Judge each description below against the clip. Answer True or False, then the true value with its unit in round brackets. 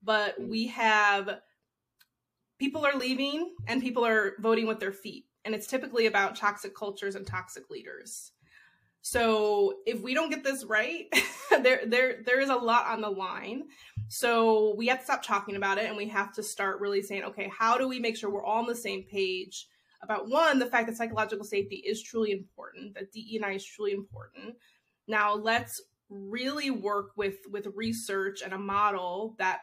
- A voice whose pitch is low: False (215 Hz)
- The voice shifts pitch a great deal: False (3.2 semitones)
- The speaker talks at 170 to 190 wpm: True (185 wpm)